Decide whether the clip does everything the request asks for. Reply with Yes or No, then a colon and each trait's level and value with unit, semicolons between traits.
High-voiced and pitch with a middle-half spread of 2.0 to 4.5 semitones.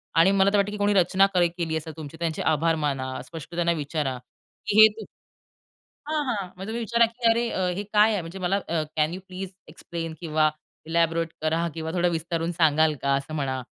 No: medium, 170 Hz; average, 3.6 semitones